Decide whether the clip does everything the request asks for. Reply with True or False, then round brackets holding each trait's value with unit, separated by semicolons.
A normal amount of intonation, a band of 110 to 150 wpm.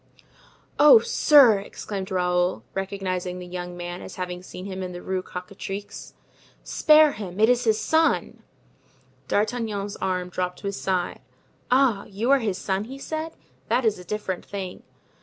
False (3.9 semitones; 160 wpm)